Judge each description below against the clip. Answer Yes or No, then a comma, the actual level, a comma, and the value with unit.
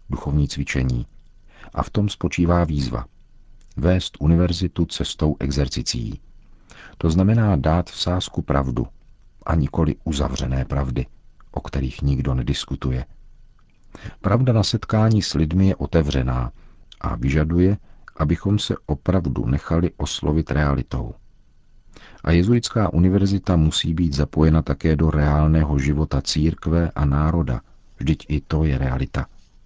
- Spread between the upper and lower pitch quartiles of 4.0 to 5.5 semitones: Yes, average, 4.3 semitones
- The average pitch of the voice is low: Yes, very low, 80 Hz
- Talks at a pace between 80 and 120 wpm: Yes, slow, 115 wpm